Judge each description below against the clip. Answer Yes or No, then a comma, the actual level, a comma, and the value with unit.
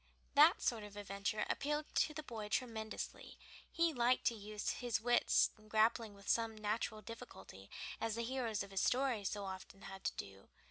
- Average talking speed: Yes, average, 190 wpm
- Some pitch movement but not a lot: Yes, average, 3.0 semitones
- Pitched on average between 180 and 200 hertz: No, high, 220 Hz